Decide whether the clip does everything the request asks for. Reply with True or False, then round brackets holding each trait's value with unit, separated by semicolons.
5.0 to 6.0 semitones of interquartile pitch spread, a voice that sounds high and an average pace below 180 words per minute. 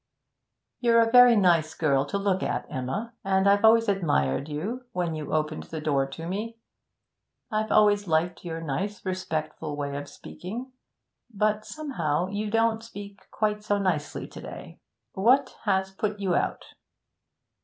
True (5.3 semitones; 195 Hz; 155 wpm)